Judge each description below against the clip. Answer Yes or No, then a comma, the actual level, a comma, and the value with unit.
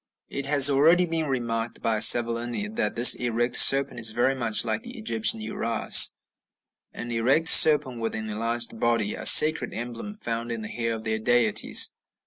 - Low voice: Yes, low, 120 Hz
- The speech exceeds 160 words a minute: Yes, average, 170 wpm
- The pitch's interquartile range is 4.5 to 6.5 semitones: No, average, 3.8 semitones